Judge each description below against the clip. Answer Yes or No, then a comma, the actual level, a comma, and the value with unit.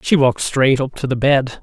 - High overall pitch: No, low, 135 Hz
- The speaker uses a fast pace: Yes, fast, 260 wpm